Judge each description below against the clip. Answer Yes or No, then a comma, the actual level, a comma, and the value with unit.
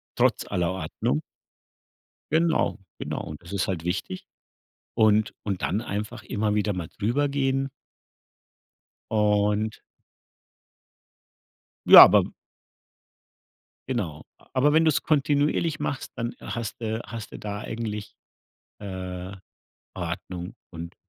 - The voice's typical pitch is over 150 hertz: No, low, 105 Hz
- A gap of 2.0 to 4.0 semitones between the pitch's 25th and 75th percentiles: No, average, 4.7 semitones